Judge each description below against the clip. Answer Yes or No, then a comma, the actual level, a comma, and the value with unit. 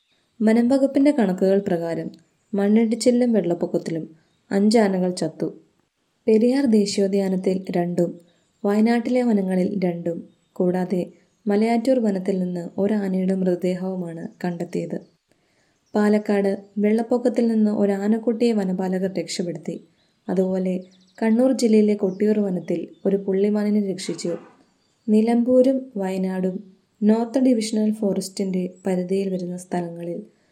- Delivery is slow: No, average, 85 wpm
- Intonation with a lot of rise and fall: No, average, 3.1 semitones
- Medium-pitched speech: No, high, 195 Hz